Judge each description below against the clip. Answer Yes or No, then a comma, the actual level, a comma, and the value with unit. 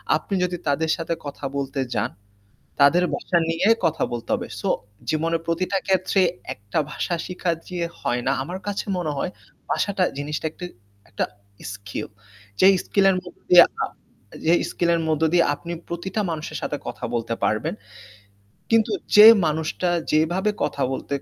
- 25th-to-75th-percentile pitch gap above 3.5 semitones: Yes, average, 4.0 semitones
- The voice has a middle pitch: Yes, medium, 165 Hz